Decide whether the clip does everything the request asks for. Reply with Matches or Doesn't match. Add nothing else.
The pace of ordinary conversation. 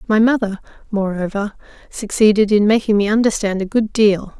Matches